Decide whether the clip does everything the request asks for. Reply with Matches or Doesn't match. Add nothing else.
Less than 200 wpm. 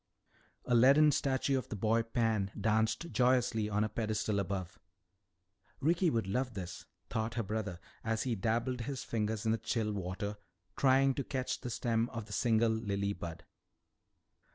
Matches